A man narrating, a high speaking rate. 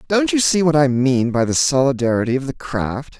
Yes: male; fast, 225 wpm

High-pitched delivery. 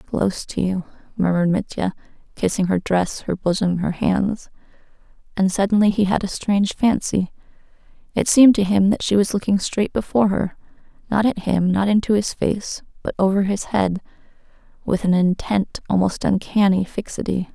Yes: high, 195 Hz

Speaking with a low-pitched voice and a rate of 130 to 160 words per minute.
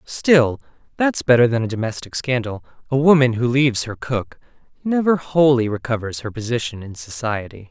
Yes: low, 125 Hz; average, 155 wpm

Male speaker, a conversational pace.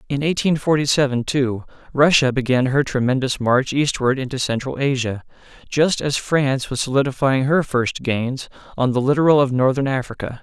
Yes: male; average, 160 wpm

